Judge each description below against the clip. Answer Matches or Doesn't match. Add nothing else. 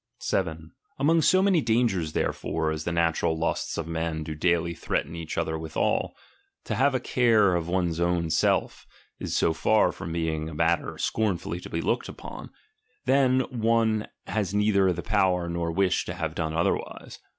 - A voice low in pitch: Matches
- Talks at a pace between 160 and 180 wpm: Matches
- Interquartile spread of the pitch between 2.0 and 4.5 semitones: Doesn't match